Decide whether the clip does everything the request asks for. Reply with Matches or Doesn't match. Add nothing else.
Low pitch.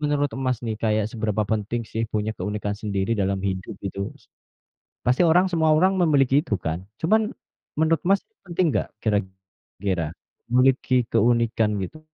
Matches